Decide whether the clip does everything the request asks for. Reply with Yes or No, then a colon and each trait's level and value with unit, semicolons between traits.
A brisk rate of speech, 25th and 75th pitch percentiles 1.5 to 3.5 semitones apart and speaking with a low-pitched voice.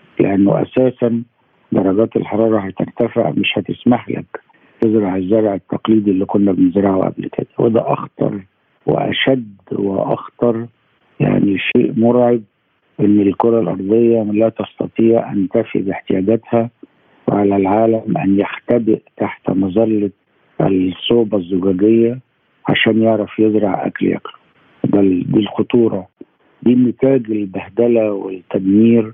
No: average, 105 wpm; average, 2.7 semitones; low, 110 Hz